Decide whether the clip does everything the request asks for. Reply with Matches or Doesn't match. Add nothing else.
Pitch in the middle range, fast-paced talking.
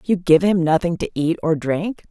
Matches